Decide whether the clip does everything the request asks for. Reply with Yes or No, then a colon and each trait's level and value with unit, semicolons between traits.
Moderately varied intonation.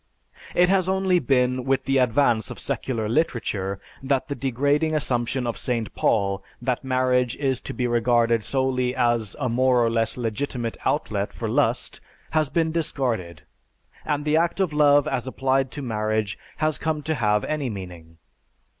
Yes: average, 3.8 semitones